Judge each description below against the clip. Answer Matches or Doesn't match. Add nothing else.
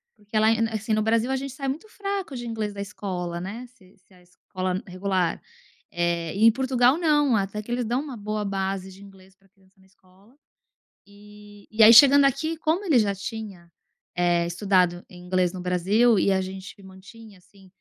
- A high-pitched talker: Matches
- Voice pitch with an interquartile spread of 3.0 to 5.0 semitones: Matches